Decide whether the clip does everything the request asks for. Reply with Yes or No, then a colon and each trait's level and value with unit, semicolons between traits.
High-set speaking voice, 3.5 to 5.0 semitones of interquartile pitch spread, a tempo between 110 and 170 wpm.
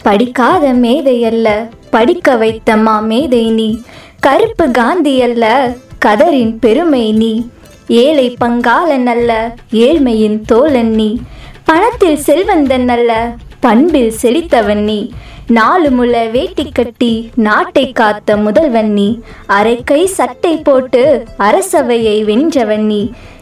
No: high, 240 Hz; average, 4.1 semitones; average, 90 wpm